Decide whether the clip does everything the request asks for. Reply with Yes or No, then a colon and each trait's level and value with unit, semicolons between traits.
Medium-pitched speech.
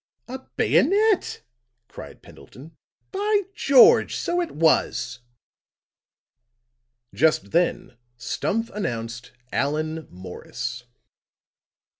Yes: medium, 160 Hz